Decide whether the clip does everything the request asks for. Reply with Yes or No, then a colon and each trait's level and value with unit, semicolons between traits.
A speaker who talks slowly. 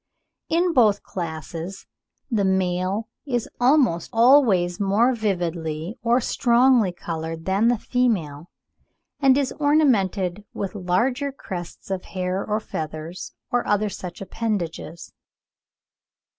Yes: slow, 110 wpm